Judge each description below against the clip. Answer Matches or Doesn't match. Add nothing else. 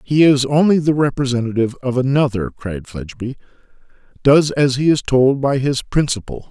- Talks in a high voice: Doesn't match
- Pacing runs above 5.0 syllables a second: Matches